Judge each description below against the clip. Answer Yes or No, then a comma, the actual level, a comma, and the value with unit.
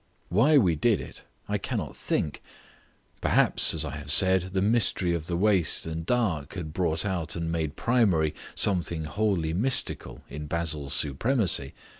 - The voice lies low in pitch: Yes, very low, 85 Hz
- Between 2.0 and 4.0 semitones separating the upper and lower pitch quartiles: No, average, 4.5 semitones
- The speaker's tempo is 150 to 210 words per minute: Yes, average, 155 wpm